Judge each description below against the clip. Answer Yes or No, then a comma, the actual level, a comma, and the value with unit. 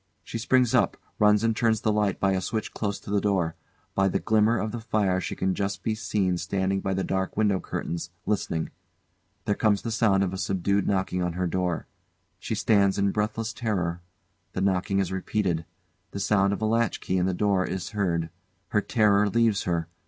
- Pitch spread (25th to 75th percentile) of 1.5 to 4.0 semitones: Yes, narrow, 2.4 semitones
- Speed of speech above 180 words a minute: Yes, average, 195 wpm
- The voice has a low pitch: Yes, low, 100 Hz